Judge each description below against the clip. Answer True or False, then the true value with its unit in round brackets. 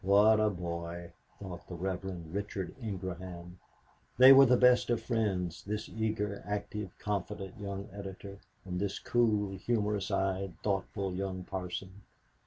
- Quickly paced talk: False (135 wpm)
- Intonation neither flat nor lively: False (2.2 semitones)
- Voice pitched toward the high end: False (100 Hz)